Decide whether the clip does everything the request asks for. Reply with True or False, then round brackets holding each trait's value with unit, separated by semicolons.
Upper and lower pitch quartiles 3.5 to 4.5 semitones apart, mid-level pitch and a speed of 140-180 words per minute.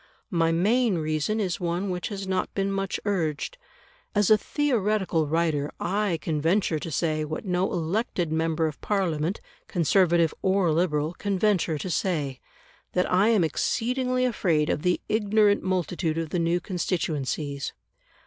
True (3.9 semitones; 180 Hz; 150 wpm)